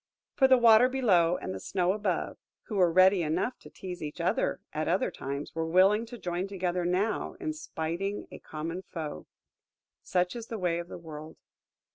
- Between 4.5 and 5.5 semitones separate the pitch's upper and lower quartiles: No, average, 4.1 semitones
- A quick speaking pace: No, average, 185 wpm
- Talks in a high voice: No, medium, 180 Hz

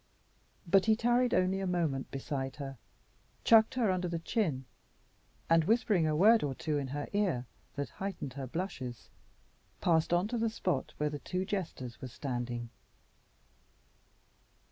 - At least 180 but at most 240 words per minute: No, average, 150 wpm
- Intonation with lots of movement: Yes, wide, 6.4 semitones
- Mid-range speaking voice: Yes, medium, 165 Hz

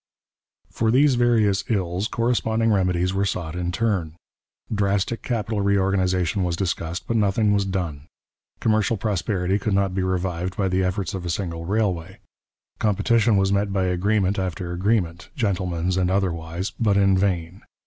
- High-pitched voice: No, very low, 95 Hz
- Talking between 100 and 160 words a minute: Yes, average, 150 wpm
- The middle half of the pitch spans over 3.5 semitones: No, narrow, 2.6 semitones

